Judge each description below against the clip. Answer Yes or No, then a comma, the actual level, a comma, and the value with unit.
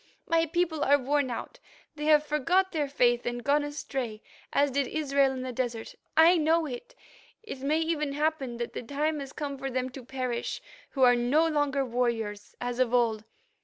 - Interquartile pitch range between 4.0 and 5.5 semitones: No, average, 3.6 semitones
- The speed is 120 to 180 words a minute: No, average, 190 wpm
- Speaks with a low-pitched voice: No, very high, 275 Hz